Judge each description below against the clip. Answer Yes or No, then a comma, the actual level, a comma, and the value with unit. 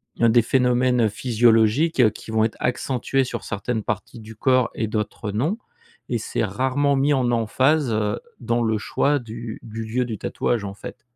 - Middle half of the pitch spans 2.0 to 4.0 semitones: Yes, average, 2.7 semitones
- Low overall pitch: Yes, low, 115 Hz